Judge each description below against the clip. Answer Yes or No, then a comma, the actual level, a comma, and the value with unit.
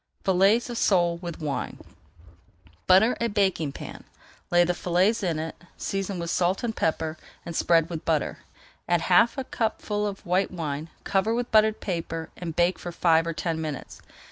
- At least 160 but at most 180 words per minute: Yes, average, 170 wpm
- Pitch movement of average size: Yes, average, 3.5 semitones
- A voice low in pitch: No, medium, 175 Hz